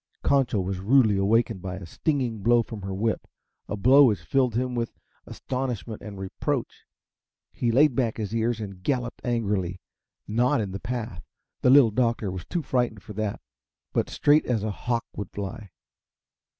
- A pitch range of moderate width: Yes, average, 3.8 semitones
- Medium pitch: No, low, 115 Hz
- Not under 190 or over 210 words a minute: No, average, 170 wpm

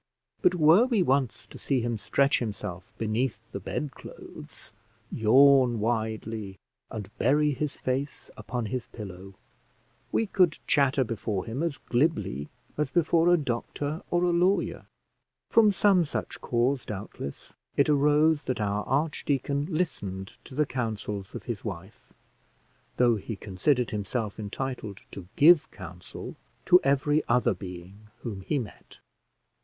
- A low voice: Yes, low, 125 Hz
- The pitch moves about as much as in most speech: No, wide, 6.0 semitones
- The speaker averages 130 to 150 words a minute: Yes, average, 140 wpm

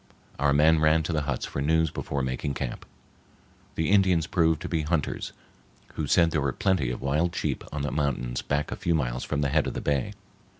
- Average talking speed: No, fast, 215 wpm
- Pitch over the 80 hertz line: No, very low, 75 Hz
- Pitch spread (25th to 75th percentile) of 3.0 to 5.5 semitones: No, narrow, 2.6 semitones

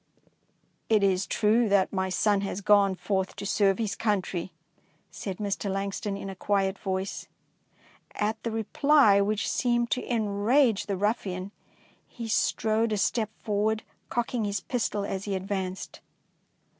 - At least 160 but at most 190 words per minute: No, average, 145 wpm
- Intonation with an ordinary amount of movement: No, narrow, 2.1 semitones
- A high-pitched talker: Yes, high, 205 Hz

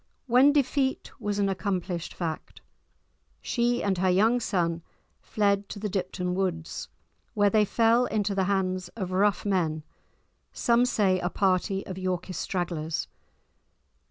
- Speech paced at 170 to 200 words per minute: No, slow, 135 wpm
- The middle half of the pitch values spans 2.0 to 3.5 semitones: Yes, average, 2.7 semitones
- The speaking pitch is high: Yes, high, 195 Hz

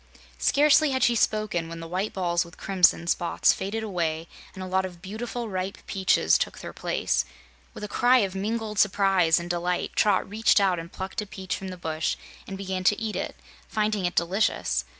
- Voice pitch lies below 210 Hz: Yes, high, 190 Hz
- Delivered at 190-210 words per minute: Yes, average, 195 wpm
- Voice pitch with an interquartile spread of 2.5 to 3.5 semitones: Yes, average, 3.2 semitones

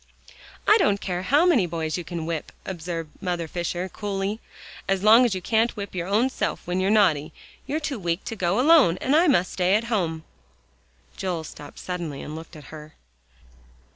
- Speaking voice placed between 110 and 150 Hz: No, medium, 185 Hz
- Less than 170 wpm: No, average, 190 wpm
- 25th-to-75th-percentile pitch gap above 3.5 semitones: Yes, average, 4.6 semitones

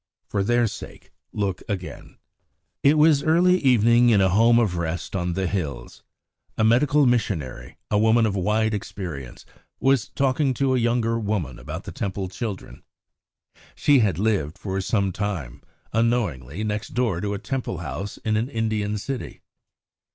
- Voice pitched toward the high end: No, low, 105 Hz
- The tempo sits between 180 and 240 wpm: No, average, 155 wpm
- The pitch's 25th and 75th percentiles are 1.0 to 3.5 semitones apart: No, average, 4.2 semitones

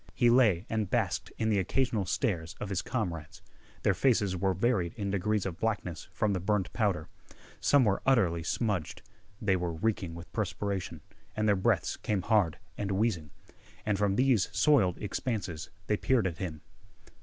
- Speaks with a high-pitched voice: No, low, 100 Hz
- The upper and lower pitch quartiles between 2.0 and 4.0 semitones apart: Yes, average, 3.7 semitones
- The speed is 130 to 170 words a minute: Yes, average, 165 wpm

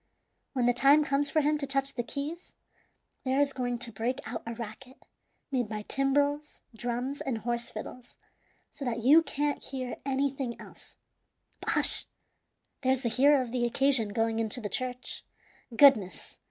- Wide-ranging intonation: No, average, 2.9 semitones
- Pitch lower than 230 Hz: No, very high, 255 Hz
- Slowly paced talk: No, average, 165 wpm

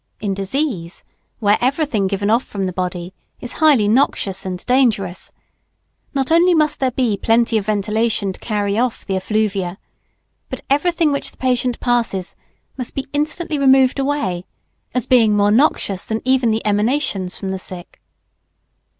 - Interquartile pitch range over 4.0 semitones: Yes, average, 5.2 semitones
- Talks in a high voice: Yes, high, 220 Hz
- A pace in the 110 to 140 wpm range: No, average, 155 wpm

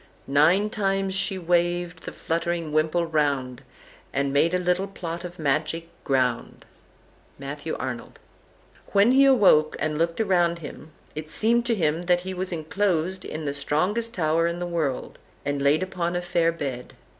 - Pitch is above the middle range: No, medium, 170 Hz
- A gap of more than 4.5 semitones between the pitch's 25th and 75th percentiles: No, average, 3.4 semitones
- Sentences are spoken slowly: No, average, 165 wpm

